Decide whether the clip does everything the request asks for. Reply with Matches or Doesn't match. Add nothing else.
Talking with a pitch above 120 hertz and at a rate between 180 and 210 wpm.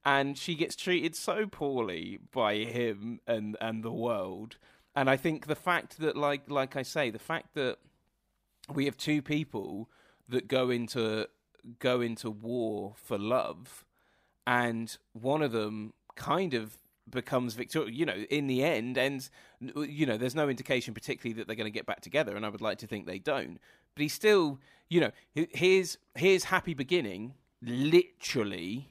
Doesn't match